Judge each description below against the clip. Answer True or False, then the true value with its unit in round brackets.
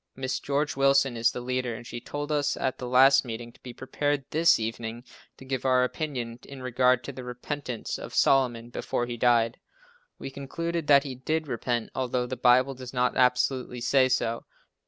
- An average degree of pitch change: False (2.3 semitones)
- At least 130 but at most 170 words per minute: False (190 wpm)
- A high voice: False (130 Hz)